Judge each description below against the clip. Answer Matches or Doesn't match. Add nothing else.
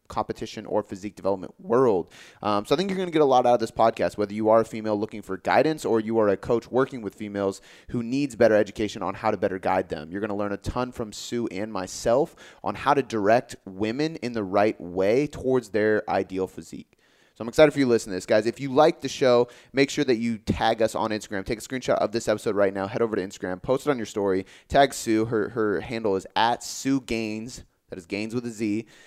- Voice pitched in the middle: Doesn't match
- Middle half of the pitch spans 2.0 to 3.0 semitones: Doesn't match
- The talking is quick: Matches